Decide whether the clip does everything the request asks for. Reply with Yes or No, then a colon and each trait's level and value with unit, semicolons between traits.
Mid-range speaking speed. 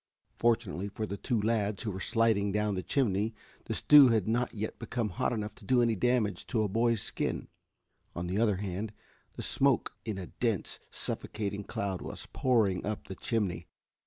Yes: average, 185 wpm